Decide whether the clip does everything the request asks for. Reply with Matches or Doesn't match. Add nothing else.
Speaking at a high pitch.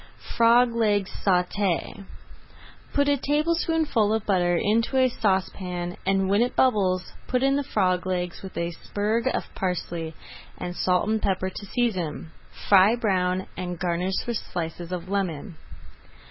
Matches